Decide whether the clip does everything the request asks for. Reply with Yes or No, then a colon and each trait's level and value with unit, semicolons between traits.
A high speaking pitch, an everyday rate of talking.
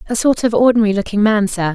No: high, 215 Hz; fast, 240 wpm